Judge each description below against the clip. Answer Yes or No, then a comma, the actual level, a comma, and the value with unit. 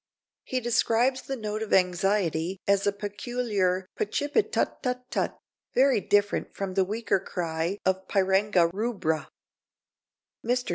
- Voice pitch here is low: No, high, 205 Hz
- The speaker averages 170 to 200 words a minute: No, average, 140 wpm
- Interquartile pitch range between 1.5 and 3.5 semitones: No, average, 4.3 semitones